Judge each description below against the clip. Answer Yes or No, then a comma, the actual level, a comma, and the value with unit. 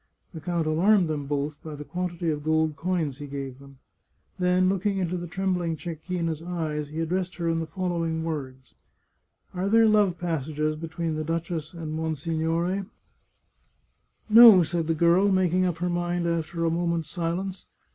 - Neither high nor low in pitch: Yes, medium, 165 Hz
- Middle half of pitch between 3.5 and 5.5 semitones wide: No, narrow, 2.4 semitones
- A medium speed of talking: Yes, average, 175 wpm